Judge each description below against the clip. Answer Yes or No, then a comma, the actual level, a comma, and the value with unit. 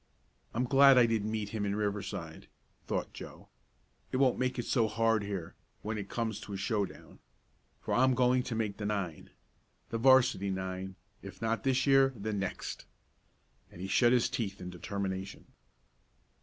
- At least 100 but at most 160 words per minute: No, average, 170 wpm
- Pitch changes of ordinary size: Yes, average, 3.9 semitones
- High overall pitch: No, low, 110 Hz